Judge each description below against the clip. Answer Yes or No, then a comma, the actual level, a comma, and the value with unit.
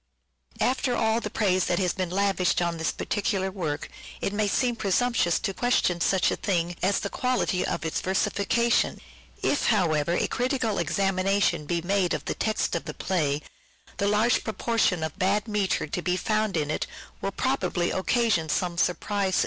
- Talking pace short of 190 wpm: Yes, average, 175 wpm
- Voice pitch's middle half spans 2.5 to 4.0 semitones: Yes, average, 3.7 semitones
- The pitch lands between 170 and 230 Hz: Yes, high, 190 Hz